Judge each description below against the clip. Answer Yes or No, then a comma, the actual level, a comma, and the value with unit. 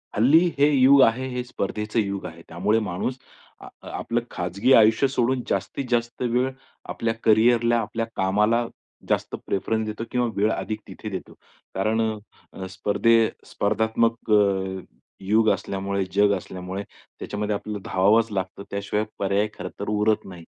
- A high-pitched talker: No, low, 110 Hz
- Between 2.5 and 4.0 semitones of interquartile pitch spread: Yes, average, 2.9 semitones